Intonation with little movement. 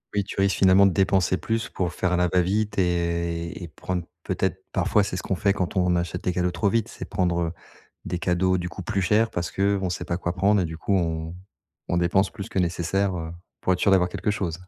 Yes: narrow, 2.1 semitones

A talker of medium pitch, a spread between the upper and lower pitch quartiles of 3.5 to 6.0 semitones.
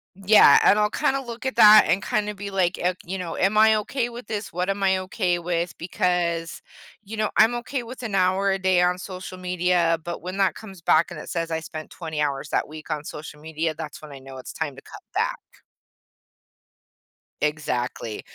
Yes: medium, 180 Hz; average, 4.0 semitones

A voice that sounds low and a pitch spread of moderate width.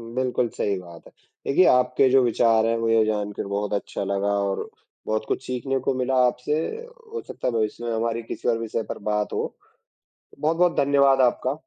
Yes: low, 115 Hz; average, 3.6 semitones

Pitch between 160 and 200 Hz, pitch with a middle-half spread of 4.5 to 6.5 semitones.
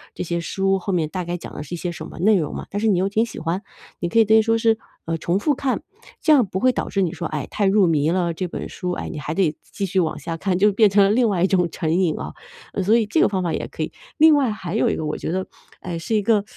No: high, 190 Hz; average, 3.8 semitones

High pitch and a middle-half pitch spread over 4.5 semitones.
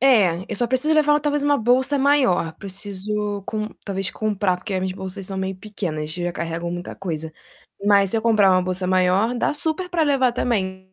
Yes: high, 200 Hz; average, 5.1 semitones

